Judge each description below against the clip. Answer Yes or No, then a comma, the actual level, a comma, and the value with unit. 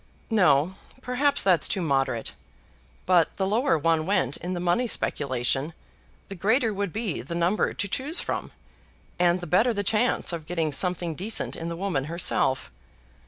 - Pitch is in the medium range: Yes, medium, 180 Hz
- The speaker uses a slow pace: No, average, 165 wpm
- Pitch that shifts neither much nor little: Yes, average, 4.1 semitones